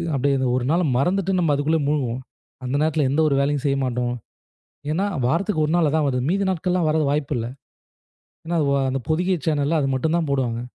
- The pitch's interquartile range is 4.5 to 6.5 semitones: No, average, 3.3 semitones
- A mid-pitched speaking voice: Yes, medium, 150 Hz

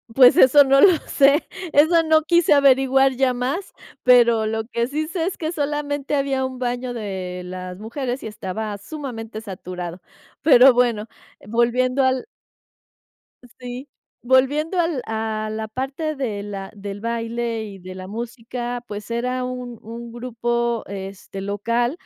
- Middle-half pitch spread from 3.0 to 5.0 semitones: Yes, average, 3.8 semitones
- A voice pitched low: No, high, 245 Hz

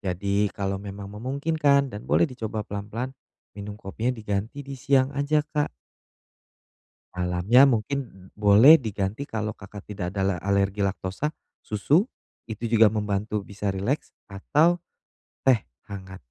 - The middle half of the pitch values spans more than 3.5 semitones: Yes, average, 5.2 semitones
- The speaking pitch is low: Yes, low, 105 Hz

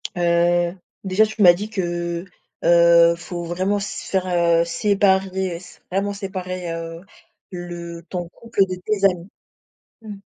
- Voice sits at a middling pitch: Yes, medium, 180 Hz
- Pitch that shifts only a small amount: Yes, narrow, 2.1 semitones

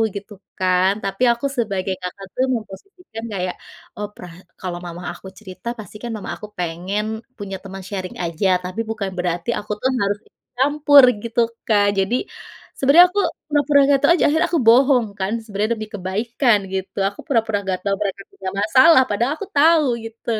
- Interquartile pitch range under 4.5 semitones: No, average, 5.0 semitones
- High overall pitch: Yes, high, 210 Hz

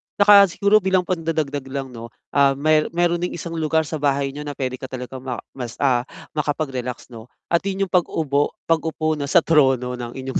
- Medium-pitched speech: Yes, medium, 145 Hz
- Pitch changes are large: No, average, 3.9 semitones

